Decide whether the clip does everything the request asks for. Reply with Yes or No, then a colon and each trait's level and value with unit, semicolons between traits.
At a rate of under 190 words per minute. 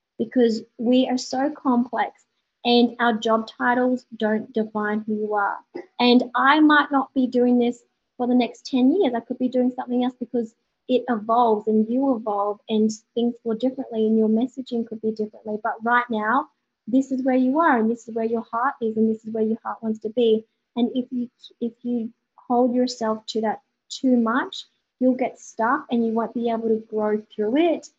No: fast, 205 wpm